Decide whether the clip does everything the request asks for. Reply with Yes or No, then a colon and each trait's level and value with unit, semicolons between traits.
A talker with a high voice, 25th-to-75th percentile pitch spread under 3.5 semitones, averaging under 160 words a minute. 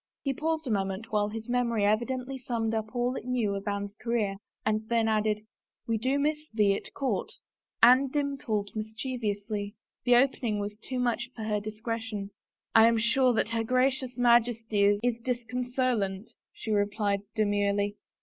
No: high, 225 Hz; average, 3.1 semitones; average, 170 wpm